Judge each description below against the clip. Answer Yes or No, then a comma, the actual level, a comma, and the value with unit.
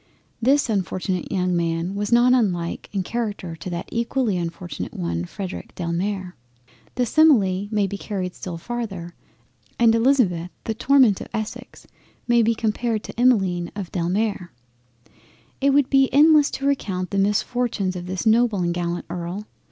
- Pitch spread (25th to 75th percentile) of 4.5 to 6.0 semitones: Yes, average, 5.0 semitones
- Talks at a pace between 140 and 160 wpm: Yes, average, 155 wpm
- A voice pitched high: Yes, high, 200 Hz